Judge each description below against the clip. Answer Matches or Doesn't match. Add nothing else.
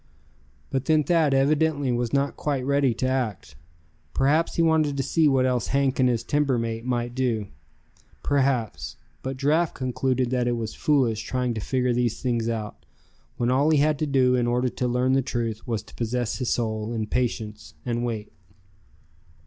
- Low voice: Matches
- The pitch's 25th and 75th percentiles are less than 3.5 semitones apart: Matches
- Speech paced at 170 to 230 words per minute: Matches